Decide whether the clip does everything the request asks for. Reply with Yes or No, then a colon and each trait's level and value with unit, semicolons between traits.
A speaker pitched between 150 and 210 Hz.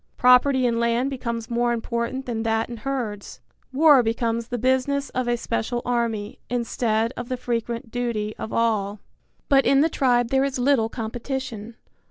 No: high, 240 Hz